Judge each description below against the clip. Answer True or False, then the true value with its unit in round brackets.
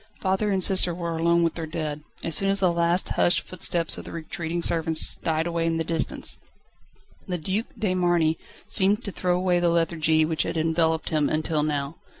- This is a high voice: False (170 Hz)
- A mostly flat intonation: True (1.9 semitones)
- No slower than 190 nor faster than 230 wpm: True (195 wpm)